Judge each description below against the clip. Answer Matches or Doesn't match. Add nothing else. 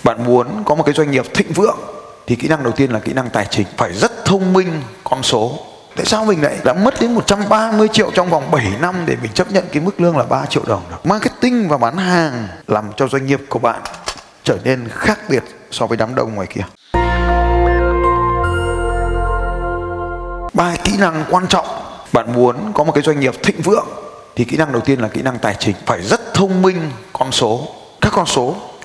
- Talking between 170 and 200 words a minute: Doesn't match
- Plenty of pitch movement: Matches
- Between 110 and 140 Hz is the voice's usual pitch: Doesn't match